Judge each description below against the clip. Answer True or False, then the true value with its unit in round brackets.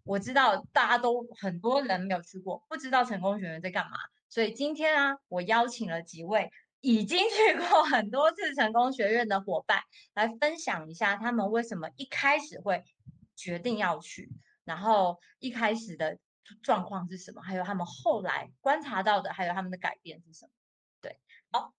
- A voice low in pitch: False (215 Hz)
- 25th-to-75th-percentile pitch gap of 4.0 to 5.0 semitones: False (5.5 semitones)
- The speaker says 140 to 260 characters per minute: False (275 characters per minute)